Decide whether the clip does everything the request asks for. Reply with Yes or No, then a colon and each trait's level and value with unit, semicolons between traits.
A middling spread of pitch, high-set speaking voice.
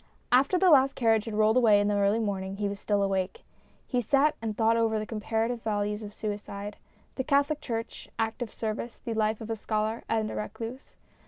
No: narrow, 2.2 semitones; high, 220 Hz